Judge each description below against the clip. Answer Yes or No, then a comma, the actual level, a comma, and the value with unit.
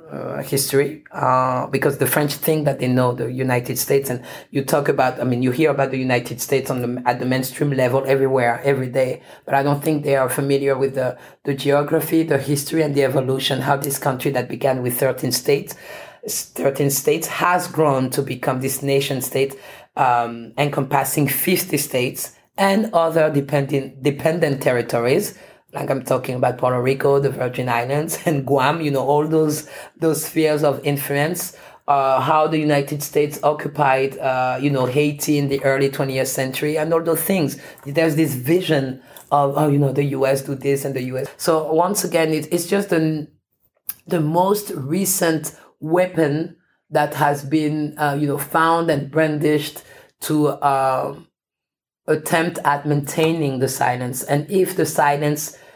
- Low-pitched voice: No, medium, 145 Hz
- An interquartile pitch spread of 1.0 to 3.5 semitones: Yes, narrow, 2.5 semitones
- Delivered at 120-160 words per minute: No, average, 170 wpm